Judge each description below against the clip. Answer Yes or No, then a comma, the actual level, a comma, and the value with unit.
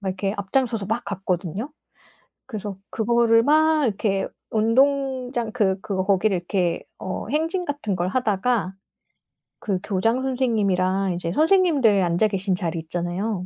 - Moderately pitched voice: No, high, 210 Hz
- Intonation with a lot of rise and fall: No, average, 4.8 semitones